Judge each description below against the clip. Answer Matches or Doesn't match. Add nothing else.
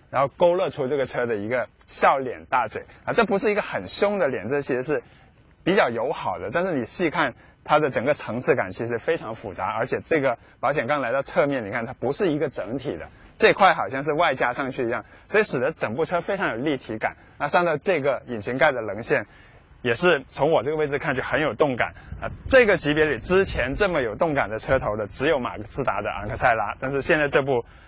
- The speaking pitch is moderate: Matches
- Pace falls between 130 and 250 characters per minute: Doesn't match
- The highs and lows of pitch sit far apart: Matches